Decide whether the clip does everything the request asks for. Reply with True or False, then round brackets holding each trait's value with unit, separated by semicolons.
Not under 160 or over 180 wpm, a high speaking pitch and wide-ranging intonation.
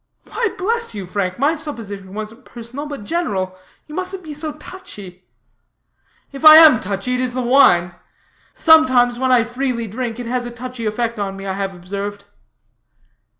True (170 wpm; 245 Hz; 6.5 semitones)